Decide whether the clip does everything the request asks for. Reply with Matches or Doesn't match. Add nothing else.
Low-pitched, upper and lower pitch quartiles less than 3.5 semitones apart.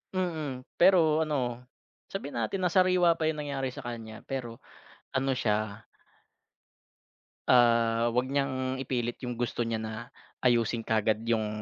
Doesn't match